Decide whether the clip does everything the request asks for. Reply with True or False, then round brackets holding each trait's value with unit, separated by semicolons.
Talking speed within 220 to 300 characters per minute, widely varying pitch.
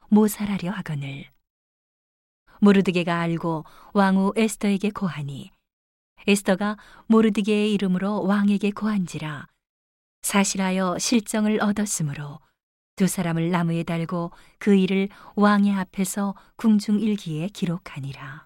False (270 characters per minute; 3.7 semitones)